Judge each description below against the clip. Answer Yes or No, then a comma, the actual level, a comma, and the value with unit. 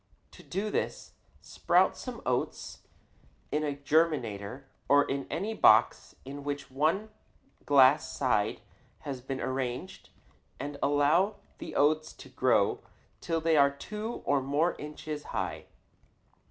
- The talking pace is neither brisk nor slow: No, slow, 125 wpm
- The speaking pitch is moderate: Yes, medium, 145 Hz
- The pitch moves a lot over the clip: No, average, 2.9 semitones